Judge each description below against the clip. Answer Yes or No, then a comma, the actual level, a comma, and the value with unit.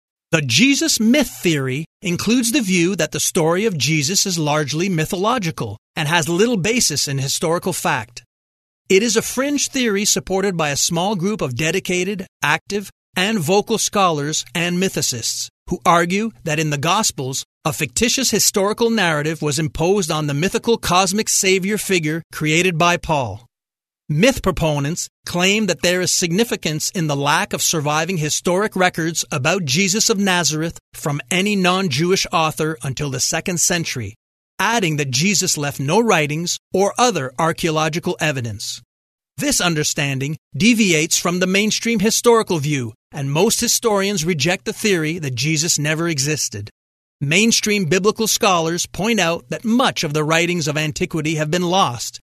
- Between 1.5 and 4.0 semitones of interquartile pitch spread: No, average, 4.5 semitones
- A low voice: No, medium, 175 Hz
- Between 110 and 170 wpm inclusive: Yes, average, 150 wpm